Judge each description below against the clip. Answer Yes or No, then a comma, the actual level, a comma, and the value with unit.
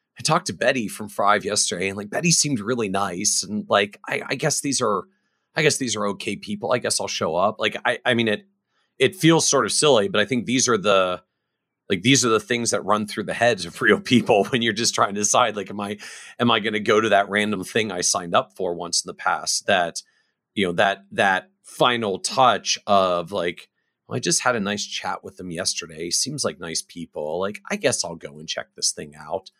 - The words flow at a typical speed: No, fast, 240 wpm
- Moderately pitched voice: No, low, 110 Hz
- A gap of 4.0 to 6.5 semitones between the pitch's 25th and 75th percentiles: Yes, average, 5.2 semitones